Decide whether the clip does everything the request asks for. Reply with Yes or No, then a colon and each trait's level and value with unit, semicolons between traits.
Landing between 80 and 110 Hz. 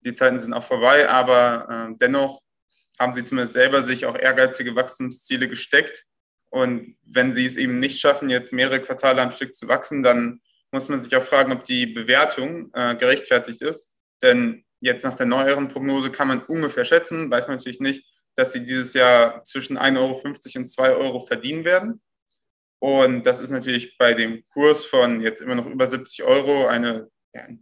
No: low, 130 Hz